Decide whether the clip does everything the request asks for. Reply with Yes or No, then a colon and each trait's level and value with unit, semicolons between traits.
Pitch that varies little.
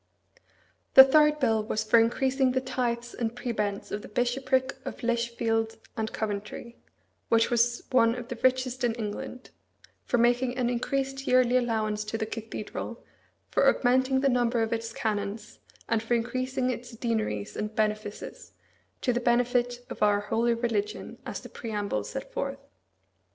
Yes: narrow, 2.3 semitones